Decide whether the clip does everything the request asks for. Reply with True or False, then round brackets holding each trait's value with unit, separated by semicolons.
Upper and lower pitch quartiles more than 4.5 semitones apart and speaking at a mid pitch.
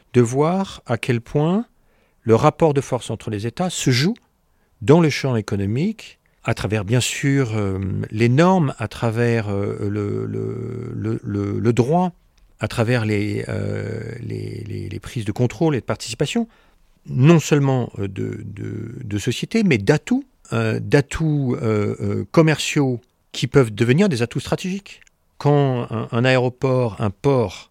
False (4.9 semitones; 120 Hz)